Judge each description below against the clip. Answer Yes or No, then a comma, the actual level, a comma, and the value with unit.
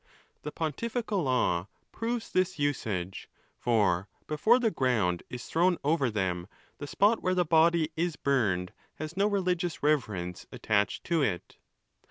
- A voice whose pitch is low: No, medium, 150 Hz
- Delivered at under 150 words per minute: Yes, average, 140 wpm